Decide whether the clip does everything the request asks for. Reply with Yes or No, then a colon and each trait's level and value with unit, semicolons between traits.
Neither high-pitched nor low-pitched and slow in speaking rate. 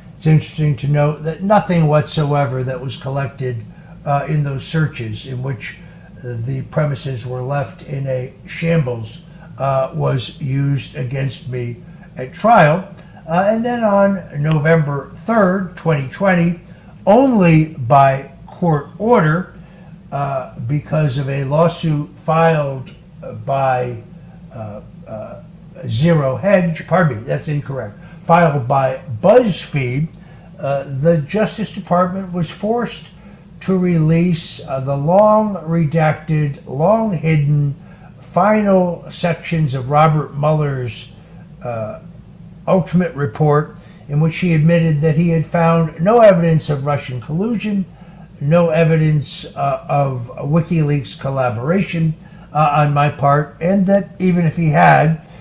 Yes: medium, 160 Hz; slow, 120 wpm